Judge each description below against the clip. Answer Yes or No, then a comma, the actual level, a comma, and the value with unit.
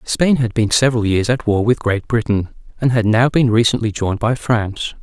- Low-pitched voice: Yes, low, 115 Hz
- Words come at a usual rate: No, fast, 215 wpm